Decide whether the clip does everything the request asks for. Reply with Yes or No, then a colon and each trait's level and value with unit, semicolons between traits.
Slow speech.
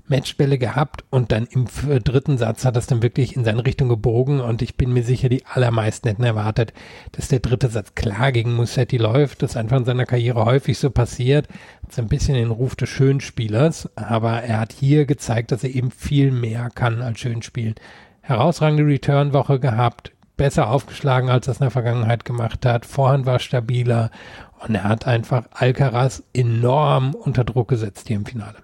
No: average, 185 wpm